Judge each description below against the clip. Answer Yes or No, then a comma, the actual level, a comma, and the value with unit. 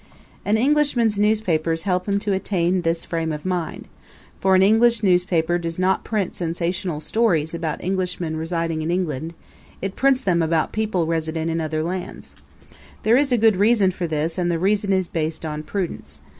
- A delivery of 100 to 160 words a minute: No, average, 175 wpm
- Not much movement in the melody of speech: No, average, 3.7 semitones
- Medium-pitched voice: Yes, medium, 180 Hz